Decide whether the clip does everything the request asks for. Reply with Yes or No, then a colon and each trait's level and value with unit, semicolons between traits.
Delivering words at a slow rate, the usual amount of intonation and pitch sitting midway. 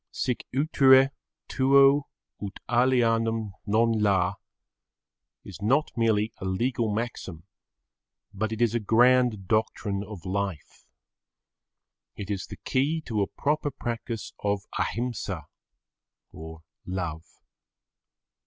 No: slow, 105 wpm; average, 4.0 semitones; low, 115 Hz